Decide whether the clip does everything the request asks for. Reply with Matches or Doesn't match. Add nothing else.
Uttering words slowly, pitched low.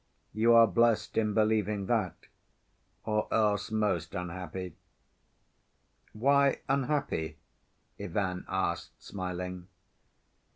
Matches